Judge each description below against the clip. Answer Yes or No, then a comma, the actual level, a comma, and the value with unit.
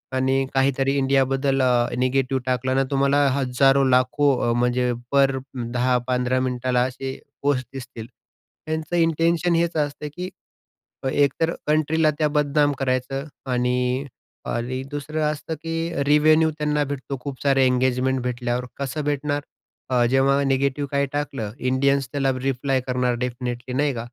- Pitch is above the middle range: No, low, 135 Hz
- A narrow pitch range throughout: Yes, narrow, 2.3 semitones